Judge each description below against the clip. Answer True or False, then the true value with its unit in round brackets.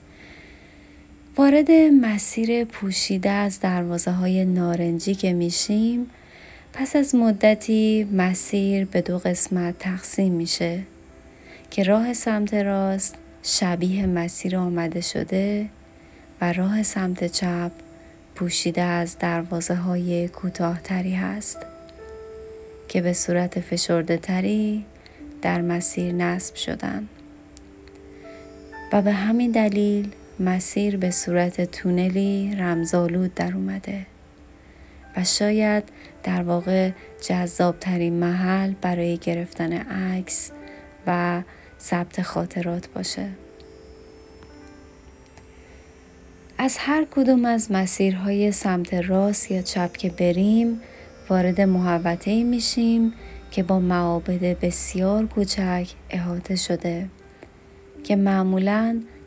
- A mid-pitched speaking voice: True (180 Hz)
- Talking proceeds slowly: True (95 wpm)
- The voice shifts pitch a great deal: False (3.0 semitones)